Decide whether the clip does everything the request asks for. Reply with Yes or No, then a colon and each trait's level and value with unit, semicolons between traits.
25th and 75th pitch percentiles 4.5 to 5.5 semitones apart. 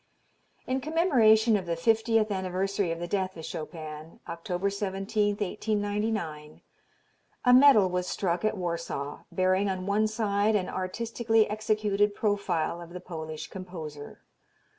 No: average, 3.8 semitones